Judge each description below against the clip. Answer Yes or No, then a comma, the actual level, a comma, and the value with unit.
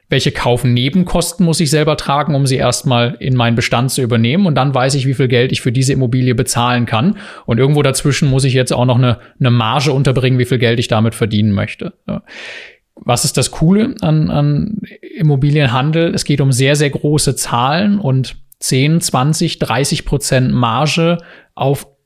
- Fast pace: No, average, 180 wpm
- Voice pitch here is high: No, low, 135 Hz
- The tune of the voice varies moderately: Yes, average, 3.6 semitones